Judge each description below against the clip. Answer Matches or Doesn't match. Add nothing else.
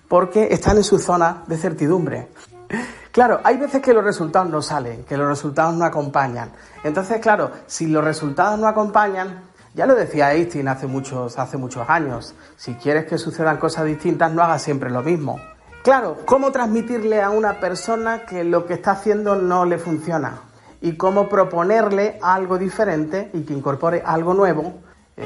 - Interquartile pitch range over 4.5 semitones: Matches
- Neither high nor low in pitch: Matches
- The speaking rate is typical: Matches